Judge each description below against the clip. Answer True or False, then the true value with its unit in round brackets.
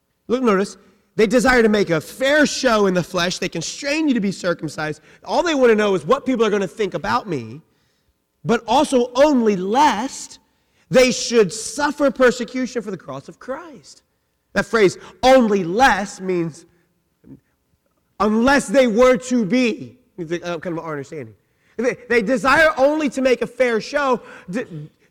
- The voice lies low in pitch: False (225 Hz)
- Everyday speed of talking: True (160 wpm)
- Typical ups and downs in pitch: False (6.7 semitones)